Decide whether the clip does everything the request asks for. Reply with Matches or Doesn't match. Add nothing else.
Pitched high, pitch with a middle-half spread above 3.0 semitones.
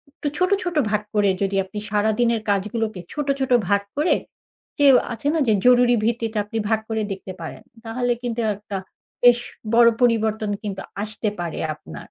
Doesn't match